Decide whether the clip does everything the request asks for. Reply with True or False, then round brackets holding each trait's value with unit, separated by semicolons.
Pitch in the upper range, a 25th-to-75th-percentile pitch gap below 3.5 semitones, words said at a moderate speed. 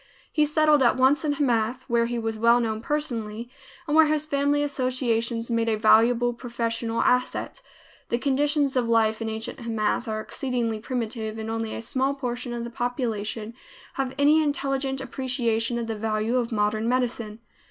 True (240 Hz; 3.0 semitones; 170 wpm)